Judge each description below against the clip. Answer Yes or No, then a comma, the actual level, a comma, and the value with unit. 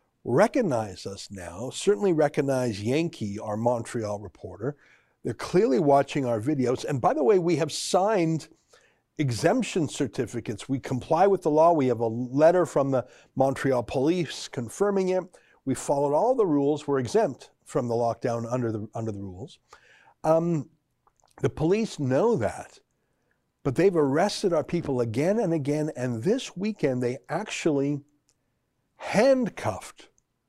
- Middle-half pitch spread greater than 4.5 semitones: Yes, average, 5.1 semitones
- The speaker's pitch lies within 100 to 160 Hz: Yes, medium, 140 Hz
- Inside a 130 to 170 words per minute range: Yes, average, 140 wpm